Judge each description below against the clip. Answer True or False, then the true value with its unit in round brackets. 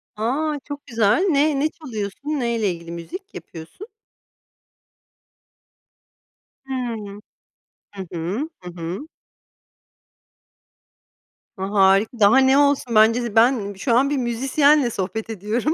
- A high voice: True (230 Hz)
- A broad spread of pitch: True (5.7 semitones)